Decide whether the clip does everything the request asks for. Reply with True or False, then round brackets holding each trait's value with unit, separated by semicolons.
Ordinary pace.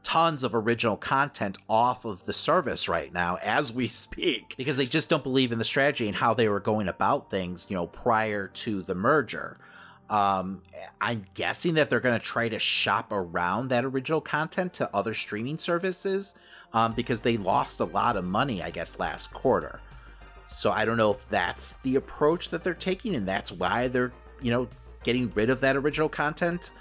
True (195 wpm)